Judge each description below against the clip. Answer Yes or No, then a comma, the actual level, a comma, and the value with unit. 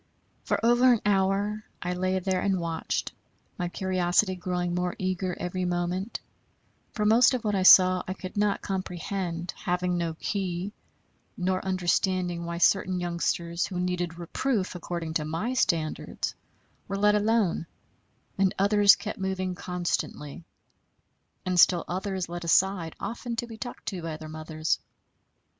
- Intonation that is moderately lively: No, narrow, 2.2 semitones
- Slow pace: No, average, 145 wpm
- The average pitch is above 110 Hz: Yes, medium, 185 Hz